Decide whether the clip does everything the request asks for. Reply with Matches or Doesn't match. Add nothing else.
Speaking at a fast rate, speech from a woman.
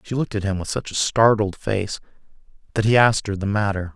Doesn't match